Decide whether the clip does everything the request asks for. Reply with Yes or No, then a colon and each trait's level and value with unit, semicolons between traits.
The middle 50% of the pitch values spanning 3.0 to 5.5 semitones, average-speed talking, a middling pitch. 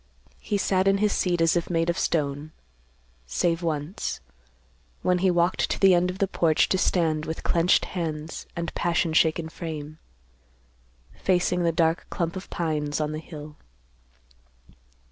No: narrow, 2.4 semitones; average, 155 wpm; medium, 170 Hz